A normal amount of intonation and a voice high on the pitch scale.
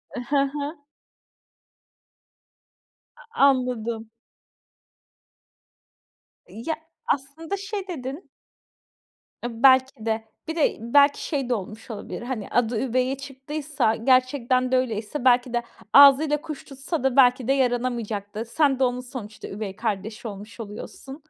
Yes: average, 3.4 semitones; very high, 255 Hz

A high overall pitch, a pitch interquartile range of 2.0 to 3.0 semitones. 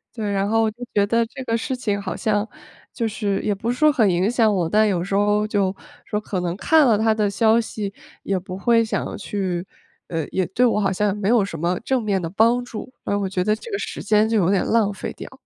Yes: high, 210 Hz; average, 2.7 semitones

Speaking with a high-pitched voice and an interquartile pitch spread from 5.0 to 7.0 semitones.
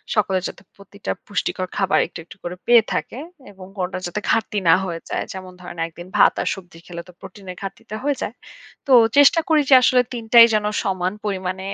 No: high, 195 Hz; average, 3.5 semitones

